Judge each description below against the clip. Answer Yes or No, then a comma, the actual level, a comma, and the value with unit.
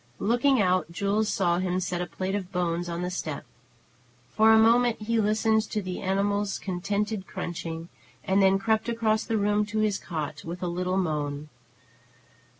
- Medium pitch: No, high, 195 Hz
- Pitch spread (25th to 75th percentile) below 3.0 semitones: No, average, 3.4 semitones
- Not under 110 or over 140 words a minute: No, average, 170 wpm